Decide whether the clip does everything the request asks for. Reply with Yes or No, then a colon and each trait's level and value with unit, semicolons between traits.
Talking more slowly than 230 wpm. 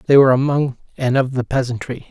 Yes: average, 200 wpm